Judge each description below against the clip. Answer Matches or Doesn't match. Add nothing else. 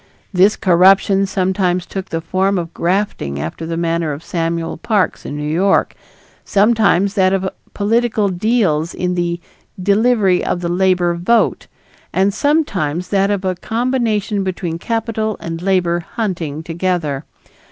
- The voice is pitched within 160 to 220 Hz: Matches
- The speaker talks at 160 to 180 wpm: Doesn't match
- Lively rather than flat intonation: Doesn't match